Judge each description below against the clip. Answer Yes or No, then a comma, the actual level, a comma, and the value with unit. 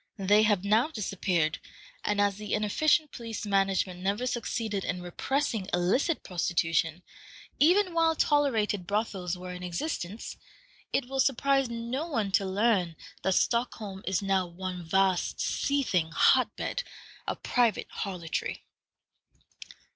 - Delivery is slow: Yes, slow, 125 wpm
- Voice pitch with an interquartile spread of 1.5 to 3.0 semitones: No, average, 5.0 semitones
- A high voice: Yes, high, 205 Hz